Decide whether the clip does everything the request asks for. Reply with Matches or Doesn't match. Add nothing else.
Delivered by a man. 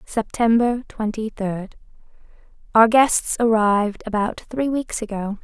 Doesn't match